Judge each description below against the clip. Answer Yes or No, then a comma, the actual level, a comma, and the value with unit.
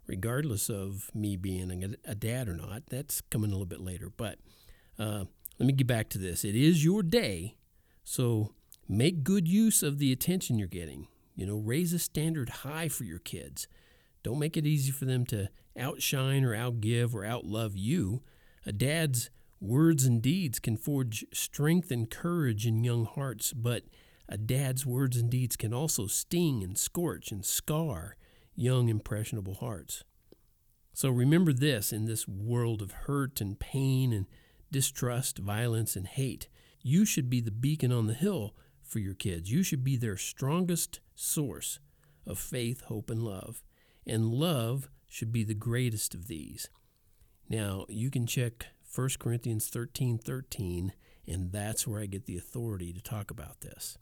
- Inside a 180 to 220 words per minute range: No, average, 170 wpm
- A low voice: Yes, low, 120 Hz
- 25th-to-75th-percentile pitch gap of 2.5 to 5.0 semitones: Yes, average, 4.6 semitones